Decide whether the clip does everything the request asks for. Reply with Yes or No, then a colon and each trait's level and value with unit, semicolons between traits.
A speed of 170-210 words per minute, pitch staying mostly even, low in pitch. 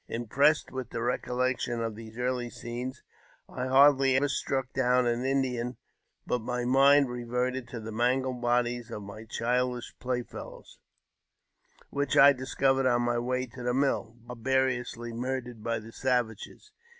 No: average, 150 wpm; narrow, 1.7 semitones; low, 125 Hz